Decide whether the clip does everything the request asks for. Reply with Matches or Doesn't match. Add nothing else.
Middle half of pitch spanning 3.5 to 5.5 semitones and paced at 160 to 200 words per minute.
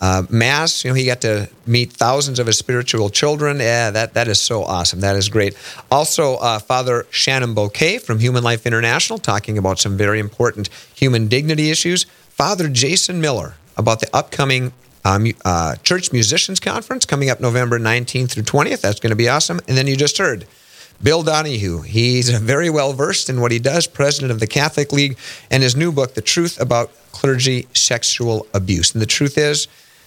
Matches